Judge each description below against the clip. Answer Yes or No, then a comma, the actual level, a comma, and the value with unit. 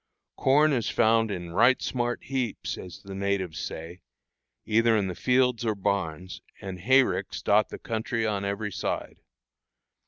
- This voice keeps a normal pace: Yes, average, 150 wpm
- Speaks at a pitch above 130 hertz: No, low, 105 Hz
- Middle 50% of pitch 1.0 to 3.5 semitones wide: No, average, 4.1 semitones